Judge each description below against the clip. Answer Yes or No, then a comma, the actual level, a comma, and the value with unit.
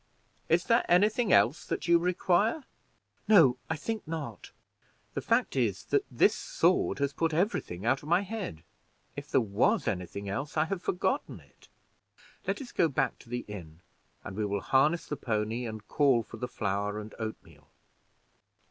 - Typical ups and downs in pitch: No, wide, 8.8 semitones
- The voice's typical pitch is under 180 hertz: Yes, medium, 140 Hz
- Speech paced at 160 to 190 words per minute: Yes, average, 175 wpm